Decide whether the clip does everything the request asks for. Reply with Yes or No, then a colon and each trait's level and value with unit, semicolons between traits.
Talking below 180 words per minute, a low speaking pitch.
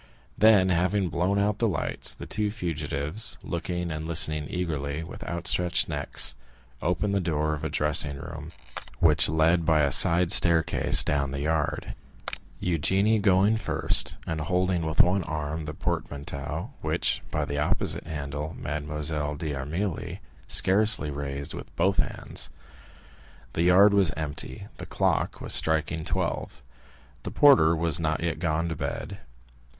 Yes: average, 145 wpm; very low, 80 Hz